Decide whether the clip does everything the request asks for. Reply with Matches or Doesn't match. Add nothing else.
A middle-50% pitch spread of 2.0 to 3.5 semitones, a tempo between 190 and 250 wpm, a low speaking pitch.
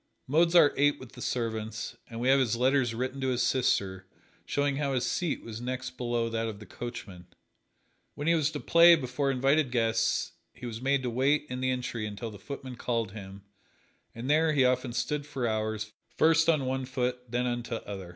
Matches